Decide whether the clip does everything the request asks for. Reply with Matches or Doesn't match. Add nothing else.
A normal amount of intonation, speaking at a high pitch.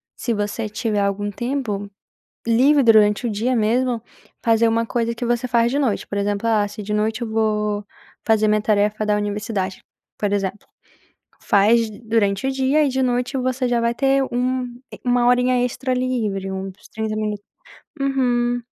Matches